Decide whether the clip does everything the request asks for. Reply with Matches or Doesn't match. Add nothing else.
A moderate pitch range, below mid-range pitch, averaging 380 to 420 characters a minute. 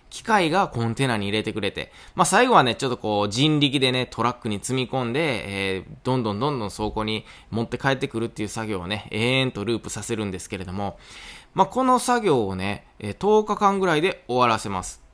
Matches